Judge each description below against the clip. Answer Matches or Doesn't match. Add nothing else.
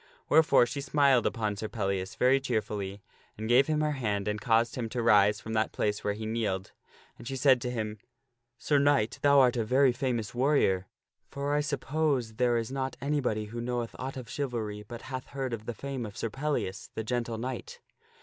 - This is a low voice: Matches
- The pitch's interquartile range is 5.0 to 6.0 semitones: Doesn't match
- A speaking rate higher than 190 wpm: Matches